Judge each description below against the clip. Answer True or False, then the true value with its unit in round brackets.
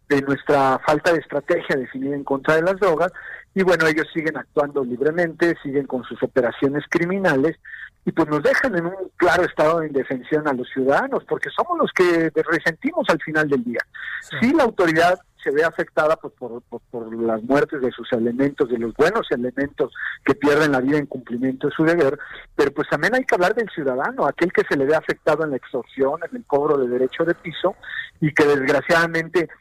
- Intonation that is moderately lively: True (3.9 semitones)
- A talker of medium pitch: True (155 Hz)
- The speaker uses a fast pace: True (205 wpm)